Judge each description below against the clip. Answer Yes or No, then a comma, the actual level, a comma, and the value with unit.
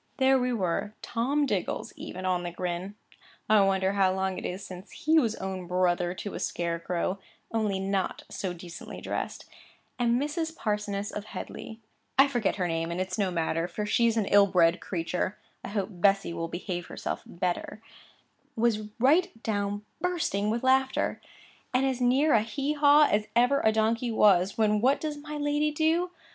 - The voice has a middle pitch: No, high, 210 Hz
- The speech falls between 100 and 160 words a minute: No, average, 170 wpm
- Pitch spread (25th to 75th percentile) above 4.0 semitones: Yes, wide, 5.4 semitones